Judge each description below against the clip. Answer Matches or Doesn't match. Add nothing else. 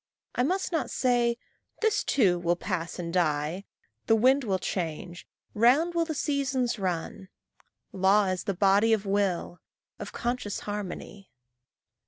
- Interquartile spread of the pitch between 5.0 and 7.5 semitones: Matches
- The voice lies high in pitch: Matches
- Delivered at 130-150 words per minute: Matches